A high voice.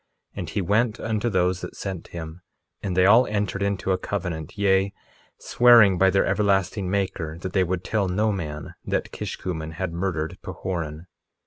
No: very low, 95 Hz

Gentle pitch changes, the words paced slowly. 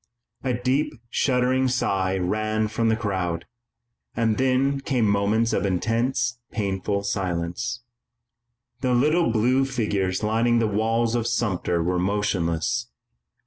No: average, 4.0 semitones; slow, 120 wpm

